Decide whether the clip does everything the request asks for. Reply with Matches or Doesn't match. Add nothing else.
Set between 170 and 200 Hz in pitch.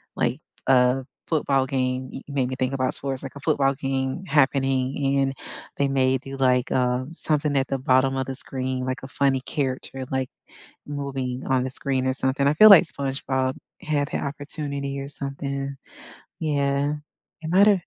Doesn't match